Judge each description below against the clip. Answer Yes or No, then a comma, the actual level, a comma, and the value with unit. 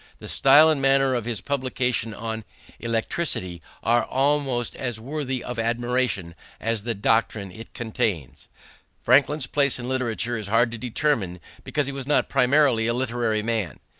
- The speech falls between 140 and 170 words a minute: Yes, average, 155 wpm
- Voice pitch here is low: Yes, low, 120 Hz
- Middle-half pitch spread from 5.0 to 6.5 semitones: No, average, 3.2 semitones